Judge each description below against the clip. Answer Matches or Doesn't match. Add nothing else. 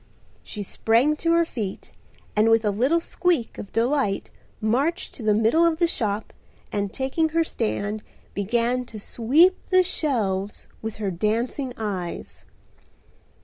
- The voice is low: Doesn't match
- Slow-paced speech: Doesn't match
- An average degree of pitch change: Doesn't match